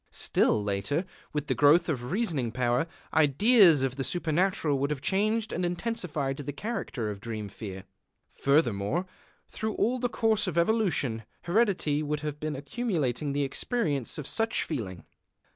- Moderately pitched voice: Yes, medium, 150 Hz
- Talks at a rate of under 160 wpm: Yes, average, 150 wpm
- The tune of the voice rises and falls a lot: Yes, wide, 6.4 semitones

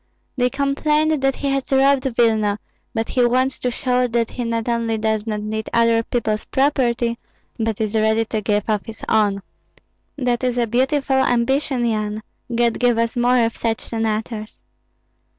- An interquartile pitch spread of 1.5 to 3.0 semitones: Yes, narrow, 2.6 semitones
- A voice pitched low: No, high, 235 Hz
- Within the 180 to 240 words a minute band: No, average, 170 wpm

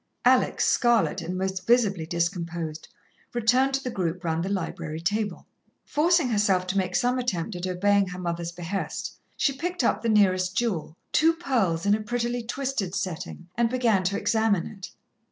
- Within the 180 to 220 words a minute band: No, average, 170 wpm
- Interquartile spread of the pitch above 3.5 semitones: Yes, average, 5.1 semitones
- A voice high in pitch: Yes, high, 200 Hz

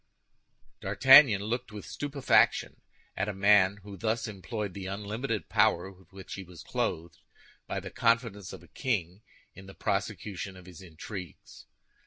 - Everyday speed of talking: Yes, average, 150 wpm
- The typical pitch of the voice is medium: No, low, 100 Hz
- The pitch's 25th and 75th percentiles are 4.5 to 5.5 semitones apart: No, average, 2.7 semitones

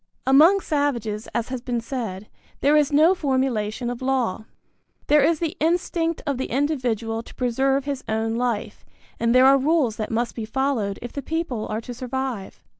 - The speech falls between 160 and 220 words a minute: Yes, average, 180 wpm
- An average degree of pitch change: Yes, average, 3.9 semitones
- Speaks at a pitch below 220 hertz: No, very high, 255 Hz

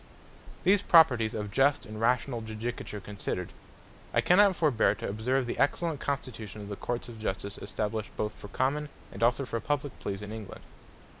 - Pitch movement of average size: Yes, average, 4.8 semitones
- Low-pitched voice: Yes, low, 115 Hz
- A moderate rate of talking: Yes, average, 170 wpm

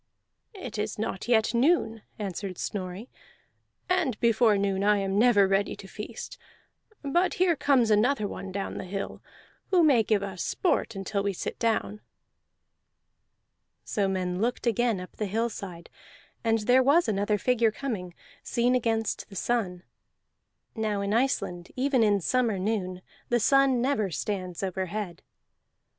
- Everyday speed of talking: Yes, average, 145 wpm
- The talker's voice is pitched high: Yes, high, 215 Hz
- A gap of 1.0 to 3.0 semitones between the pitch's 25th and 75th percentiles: No, average, 3.7 semitones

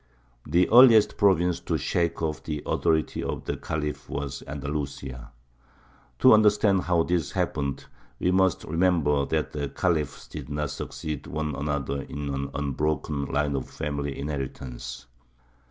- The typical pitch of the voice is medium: No, very low, 75 Hz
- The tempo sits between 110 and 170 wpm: Yes, average, 140 wpm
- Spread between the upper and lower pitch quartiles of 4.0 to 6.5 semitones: No, average, 3.3 semitones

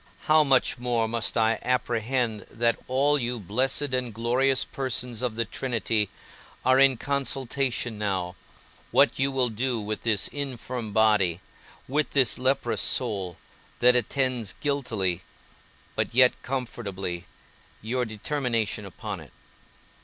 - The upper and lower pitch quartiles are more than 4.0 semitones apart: No, average, 3.3 semitones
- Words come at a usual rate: No, slow, 125 wpm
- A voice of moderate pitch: No, low, 120 Hz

